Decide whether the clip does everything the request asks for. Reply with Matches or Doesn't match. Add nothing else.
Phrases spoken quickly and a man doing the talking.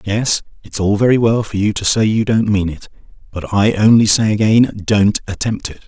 Doesn't match